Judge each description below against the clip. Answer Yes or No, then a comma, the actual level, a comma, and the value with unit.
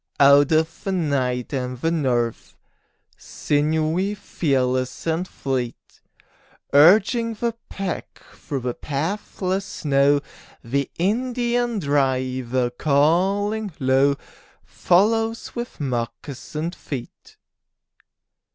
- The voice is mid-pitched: Yes, medium, 150 Hz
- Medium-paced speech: No, slow, 85 wpm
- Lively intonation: Yes, wide, 6.8 semitones